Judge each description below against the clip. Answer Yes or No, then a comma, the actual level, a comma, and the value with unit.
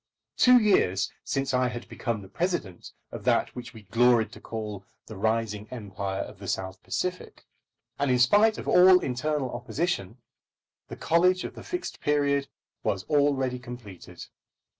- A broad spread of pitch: Yes, wide, 5.9 semitones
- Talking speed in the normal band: Yes, average, 155 wpm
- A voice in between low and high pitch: No, low, 125 Hz